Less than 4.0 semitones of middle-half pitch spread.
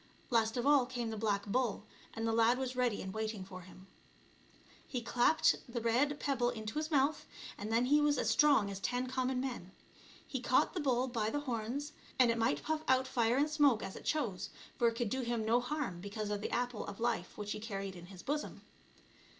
Yes: average, 3.4 semitones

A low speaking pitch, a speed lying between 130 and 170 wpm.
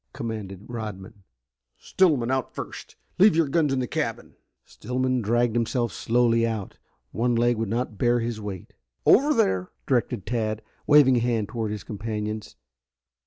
Yes: low, 115 Hz; average, 150 wpm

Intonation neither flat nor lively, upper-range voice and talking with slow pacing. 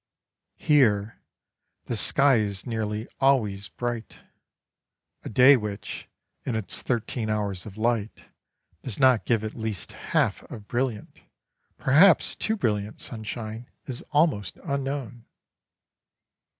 No: average, 3.7 semitones; low, 115 Hz; slow, 110 wpm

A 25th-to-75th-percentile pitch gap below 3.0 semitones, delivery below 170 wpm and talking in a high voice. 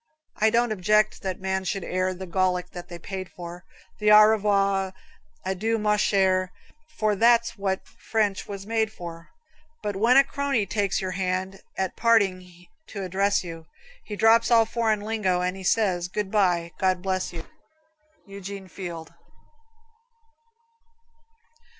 Yes: narrow, 2.5 semitones; average, 145 wpm; high, 195 Hz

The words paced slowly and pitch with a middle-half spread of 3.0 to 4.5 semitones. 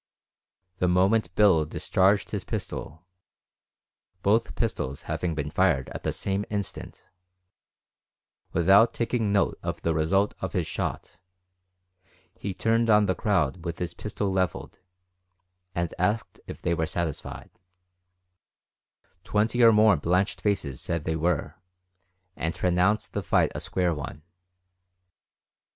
Yes: slow, 125 wpm; average, 4.0 semitones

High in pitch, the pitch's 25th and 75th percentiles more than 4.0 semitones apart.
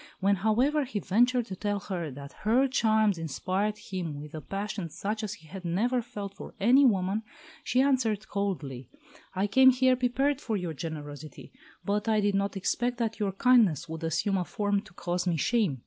Yes: high, 205 Hz; average, 4.9 semitones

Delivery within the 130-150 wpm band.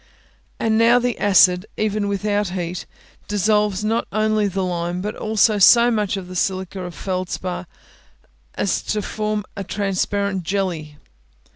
Yes: average, 145 wpm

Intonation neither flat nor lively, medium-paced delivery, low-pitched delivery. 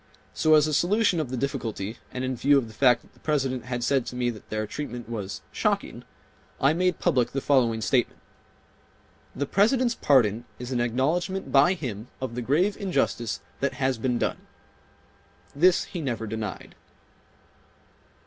Yes: average, 4.5 semitones; average, 170 wpm; low, 130 Hz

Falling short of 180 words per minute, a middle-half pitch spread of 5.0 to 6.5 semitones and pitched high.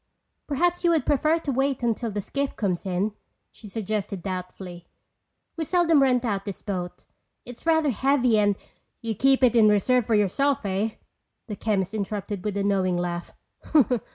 Yes: average, 165 wpm; wide, 5.5 semitones; high, 215 Hz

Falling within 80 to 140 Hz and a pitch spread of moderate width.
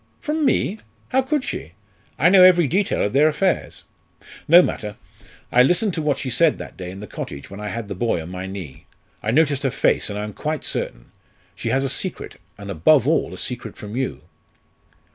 No: low, 135 Hz; wide, 8.6 semitones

